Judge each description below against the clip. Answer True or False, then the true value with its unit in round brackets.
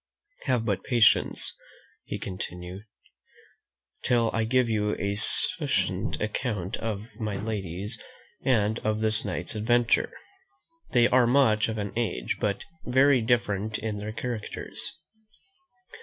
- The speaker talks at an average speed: False (120 wpm)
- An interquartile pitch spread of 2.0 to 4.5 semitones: True (2.7 semitones)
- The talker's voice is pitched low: True (110 Hz)